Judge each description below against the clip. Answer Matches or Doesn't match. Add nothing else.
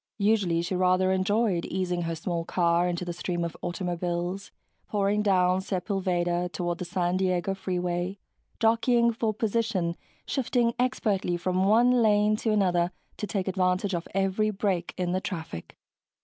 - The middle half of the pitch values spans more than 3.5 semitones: Doesn't match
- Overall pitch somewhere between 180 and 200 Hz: Matches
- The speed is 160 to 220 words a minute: Doesn't match